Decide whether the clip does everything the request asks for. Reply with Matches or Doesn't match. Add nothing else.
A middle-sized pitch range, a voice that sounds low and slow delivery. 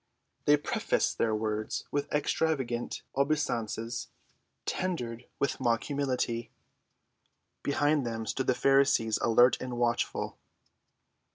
Matches